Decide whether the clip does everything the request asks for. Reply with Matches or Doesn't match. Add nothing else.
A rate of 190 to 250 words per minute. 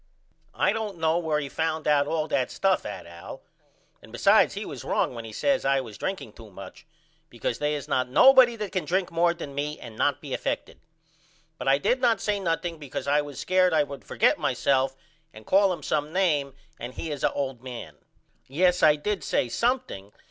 Matches